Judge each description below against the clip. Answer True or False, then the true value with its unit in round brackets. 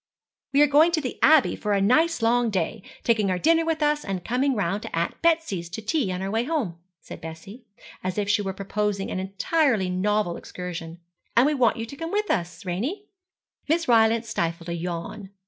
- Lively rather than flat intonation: True (7.4 semitones)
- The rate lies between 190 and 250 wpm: True (205 wpm)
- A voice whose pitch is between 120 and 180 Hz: False (215 Hz)